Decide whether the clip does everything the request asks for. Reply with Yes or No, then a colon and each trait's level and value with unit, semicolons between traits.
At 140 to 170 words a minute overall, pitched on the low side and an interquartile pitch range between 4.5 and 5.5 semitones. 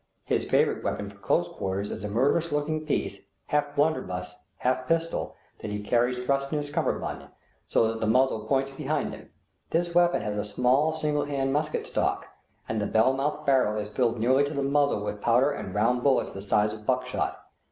No: average, 195 wpm; low, 130 Hz; average, 4.9 semitones